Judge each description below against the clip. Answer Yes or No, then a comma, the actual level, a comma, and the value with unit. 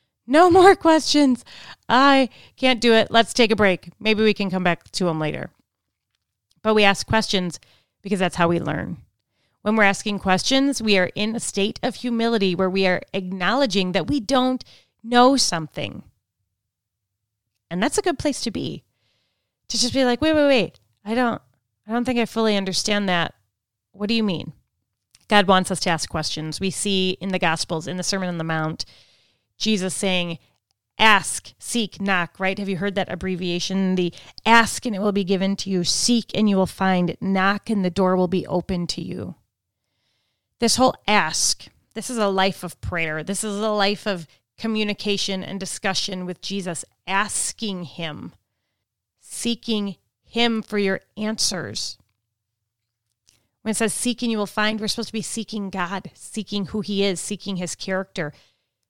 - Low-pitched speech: No, high, 190 Hz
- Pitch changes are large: Yes, wide, 5.9 semitones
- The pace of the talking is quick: No, average, 175 wpm